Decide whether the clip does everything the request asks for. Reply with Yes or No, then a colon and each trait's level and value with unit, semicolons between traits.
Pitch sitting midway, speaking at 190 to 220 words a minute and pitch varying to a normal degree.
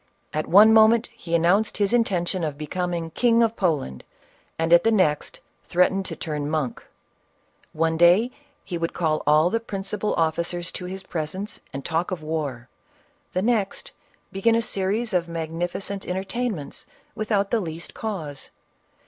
No: medium, 180 Hz; average, 155 wpm; average, 4.3 semitones